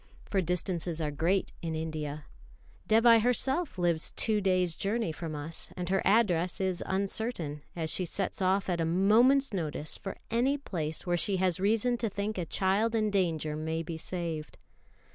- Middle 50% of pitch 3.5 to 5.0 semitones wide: Yes, average, 4.5 semitones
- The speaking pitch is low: No, medium, 185 Hz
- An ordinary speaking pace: Yes, average, 170 wpm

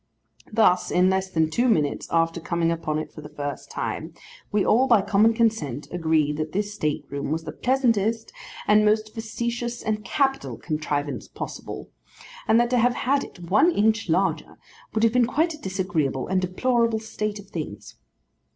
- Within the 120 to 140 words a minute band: No, average, 175 wpm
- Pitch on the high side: Yes, high, 205 Hz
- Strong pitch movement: Yes, wide, 6.0 semitones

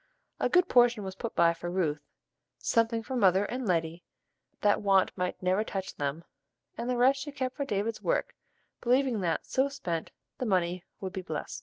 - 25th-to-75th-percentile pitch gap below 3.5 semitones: No, wide, 5.4 semitones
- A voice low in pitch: No, high, 205 Hz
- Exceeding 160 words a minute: Yes, average, 185 wpm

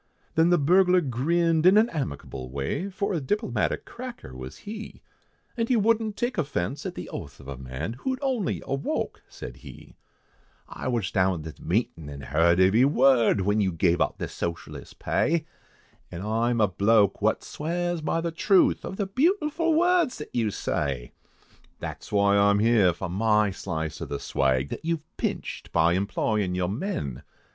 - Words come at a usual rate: Yes, average, 180 wpm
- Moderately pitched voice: No, low, 115 Hz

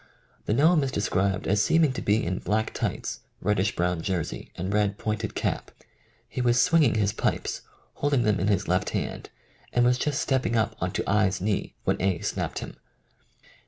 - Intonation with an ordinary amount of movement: Yes, average, 4.2 semitones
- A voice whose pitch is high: No, low, 105 Hz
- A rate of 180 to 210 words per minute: Yes, average, 190 wpm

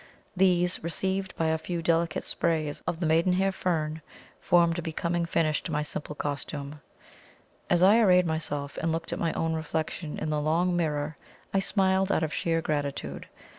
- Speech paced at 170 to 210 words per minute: Yes, average, 175 wpm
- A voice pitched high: No, medium, 165 Hz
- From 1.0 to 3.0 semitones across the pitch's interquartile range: Yes, narrow, 2.4 semitones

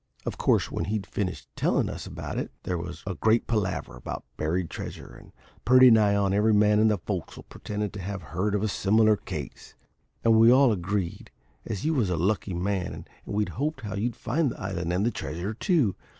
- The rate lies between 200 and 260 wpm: Yes, fast, 205 wpm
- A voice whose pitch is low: Yes, low, 105 Hz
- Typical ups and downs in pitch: Yes, average, 3.1 semitones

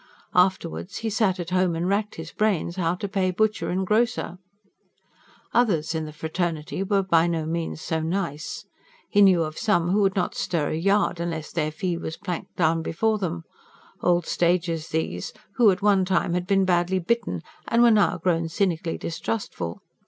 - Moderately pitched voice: Yes, medium, 180 Hz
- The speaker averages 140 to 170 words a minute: No, average, 180 wpm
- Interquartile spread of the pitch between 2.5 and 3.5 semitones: Yes, average, 3.2 semitones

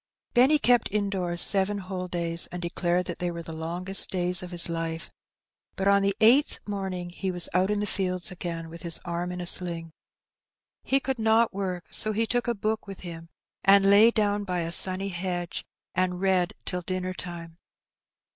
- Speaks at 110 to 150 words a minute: No, average, 190 wpm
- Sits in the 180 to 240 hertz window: Yes, medium, 185 Hz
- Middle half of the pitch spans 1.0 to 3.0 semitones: Yes, narrow, 2.5 semitones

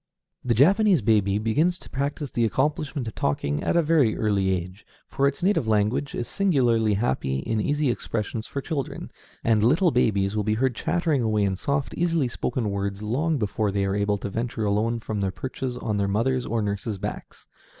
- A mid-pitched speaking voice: No, low, 115 Hz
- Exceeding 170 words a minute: Yes, average, 190 wpm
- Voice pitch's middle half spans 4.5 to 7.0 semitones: Yes, average, 5.2 semitones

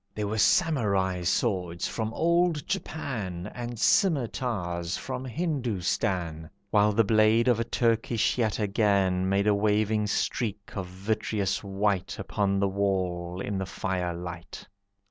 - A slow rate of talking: Yes, slow, 125 wpm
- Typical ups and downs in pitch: Yes, average, 3.5 semitones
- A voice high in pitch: No, low, 100 Hz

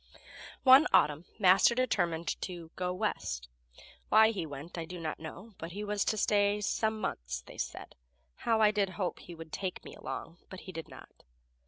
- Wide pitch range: No, average, 4.2 semitones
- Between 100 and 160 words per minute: No, average, 185 wpm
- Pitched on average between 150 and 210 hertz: Yes, medium, 185 Hz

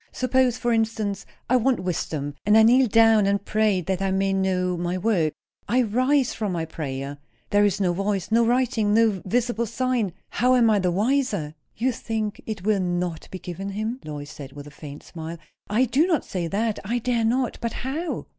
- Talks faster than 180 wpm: Yes, average, 200 wpm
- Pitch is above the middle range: Yes, high, 210 Hz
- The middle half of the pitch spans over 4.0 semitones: Yes, average, 4.6 semitones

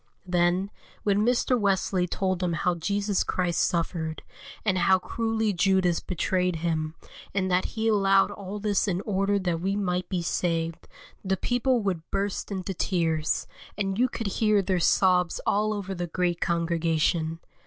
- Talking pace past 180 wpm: No, average, 155 wpm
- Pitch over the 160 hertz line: Yes, medium, 185 Hz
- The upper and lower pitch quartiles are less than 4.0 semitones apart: Yes, narrow, 2.6 semitones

